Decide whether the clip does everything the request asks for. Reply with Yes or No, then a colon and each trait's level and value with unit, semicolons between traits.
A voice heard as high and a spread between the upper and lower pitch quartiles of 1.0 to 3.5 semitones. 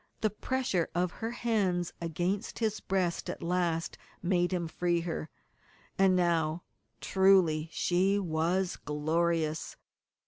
No: medium, 175 Hz; narrow, 2.5 semitones